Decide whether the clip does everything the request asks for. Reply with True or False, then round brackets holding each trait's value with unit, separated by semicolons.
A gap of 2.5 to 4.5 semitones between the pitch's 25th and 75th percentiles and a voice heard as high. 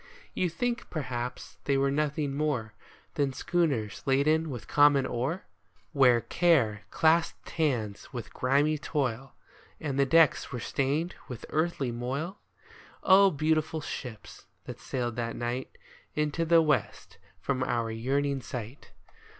False (4.2 semitones; 140 Hz)